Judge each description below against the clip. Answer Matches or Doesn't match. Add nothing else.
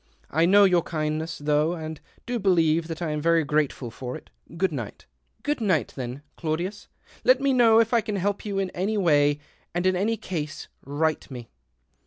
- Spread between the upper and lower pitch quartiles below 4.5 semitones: Doesn't match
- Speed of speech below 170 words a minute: Doesn't match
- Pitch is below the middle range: Doesn't match